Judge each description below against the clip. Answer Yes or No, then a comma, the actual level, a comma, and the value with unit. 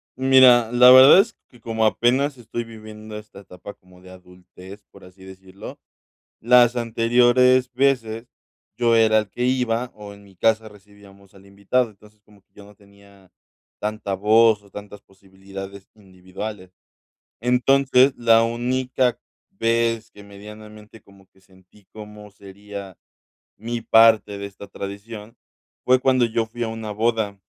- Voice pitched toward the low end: Yes, low, 110 Hz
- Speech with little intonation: No, average, 3.0 semitones